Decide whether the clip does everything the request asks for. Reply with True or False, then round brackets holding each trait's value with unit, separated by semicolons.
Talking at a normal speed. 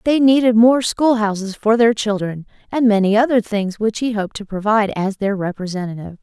True (195 wpm)